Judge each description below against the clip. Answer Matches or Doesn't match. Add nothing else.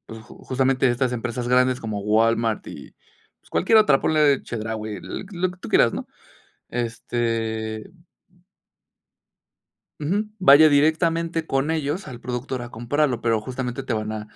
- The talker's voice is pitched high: Doesn't match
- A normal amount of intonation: Matches